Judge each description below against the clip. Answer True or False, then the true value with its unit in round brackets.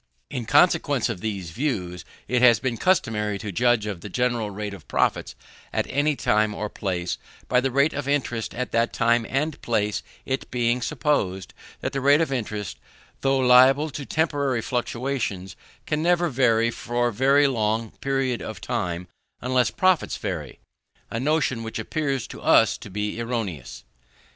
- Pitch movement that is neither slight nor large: True (4.4 semitones)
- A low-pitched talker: True (120 Hz)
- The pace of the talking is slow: False (165 wpm)